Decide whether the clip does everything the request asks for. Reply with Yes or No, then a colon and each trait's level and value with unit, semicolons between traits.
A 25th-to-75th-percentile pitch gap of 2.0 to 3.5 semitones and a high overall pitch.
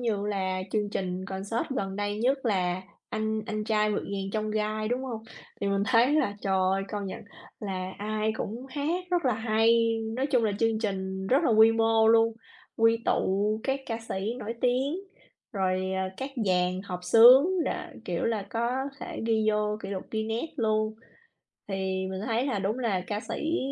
Yes: average, 2.9 semitones; high, 215 Hz